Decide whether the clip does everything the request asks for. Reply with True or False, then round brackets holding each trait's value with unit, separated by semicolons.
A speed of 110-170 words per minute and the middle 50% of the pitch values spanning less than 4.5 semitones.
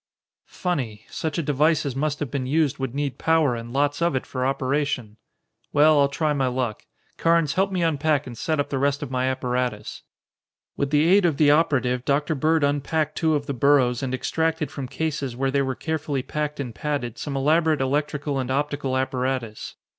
False (195 wpm; 2.8 semitones)